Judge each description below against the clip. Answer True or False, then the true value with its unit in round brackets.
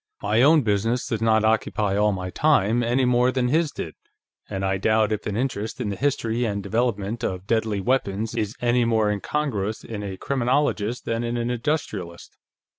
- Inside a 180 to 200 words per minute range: True (185 wpm)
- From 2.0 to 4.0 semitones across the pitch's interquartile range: True (3.2 semitones)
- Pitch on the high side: False (110 Hz)